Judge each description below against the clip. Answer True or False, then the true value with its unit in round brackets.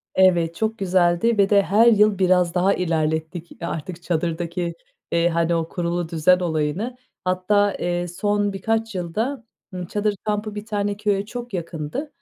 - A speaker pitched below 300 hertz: True (185 Hz)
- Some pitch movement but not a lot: True (3.5 semitones)